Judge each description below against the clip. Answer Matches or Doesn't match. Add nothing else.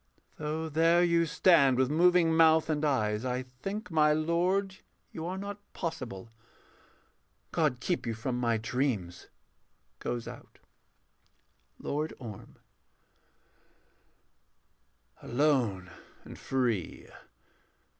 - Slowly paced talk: Matches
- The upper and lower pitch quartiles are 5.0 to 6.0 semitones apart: Matches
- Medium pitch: Matches